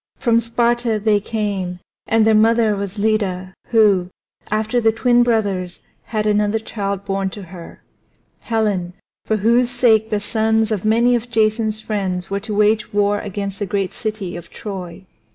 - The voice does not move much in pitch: Yes, narrow, 2.1 semitones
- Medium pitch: No, high, 215 Hz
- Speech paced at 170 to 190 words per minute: No, average, 160 wpm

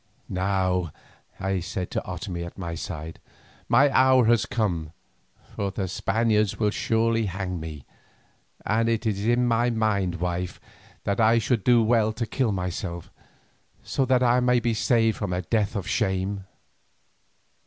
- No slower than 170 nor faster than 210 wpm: No, average, 155 wpm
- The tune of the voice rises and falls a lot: No, average, 3.9 semitones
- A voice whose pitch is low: Yes, low, 105 Hz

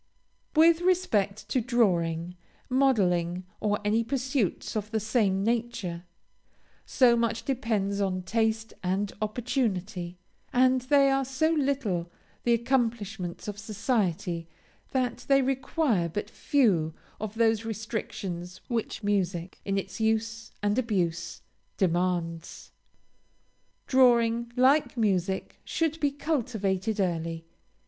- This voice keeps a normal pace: No, slow, 110 wpm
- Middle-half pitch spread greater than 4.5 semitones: Yes, average, 5.2 semitones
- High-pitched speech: Yes, high, 220 Hz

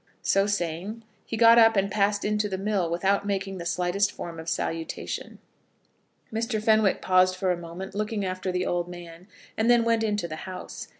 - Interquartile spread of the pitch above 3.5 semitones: No, average, 3.1 semitones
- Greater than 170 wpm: Yes, average, 185 wpm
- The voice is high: Yes, high, 195 Hz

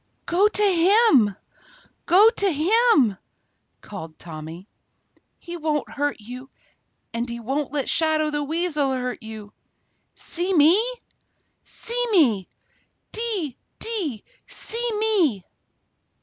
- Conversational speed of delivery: No, slow, 105 wpm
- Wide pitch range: Yes, wide, 8.3 semitones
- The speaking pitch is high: Yes, very high, 300 Hz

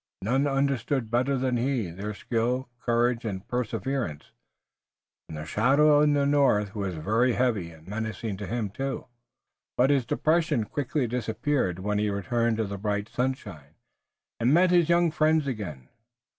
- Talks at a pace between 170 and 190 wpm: No, average, 155 wpm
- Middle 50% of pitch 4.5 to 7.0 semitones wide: Yes, average, 4.8 semitones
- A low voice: Yes, low, 120 Hz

